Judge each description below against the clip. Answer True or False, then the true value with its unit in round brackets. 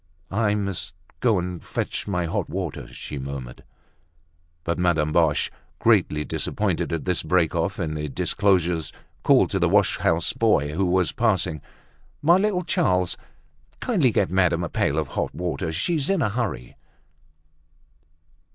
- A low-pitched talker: True (90 Hz)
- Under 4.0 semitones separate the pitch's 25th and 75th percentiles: False (4.7 semitones)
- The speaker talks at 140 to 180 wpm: True (150 wpm)